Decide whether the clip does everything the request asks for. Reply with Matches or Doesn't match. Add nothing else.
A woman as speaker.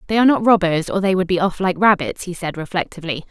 Matches